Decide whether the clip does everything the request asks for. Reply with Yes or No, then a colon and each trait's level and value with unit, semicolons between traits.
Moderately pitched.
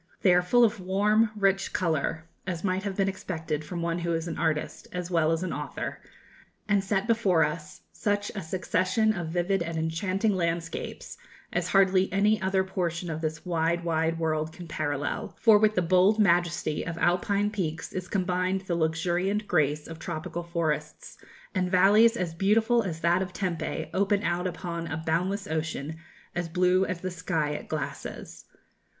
Yes: medium, 180 Hz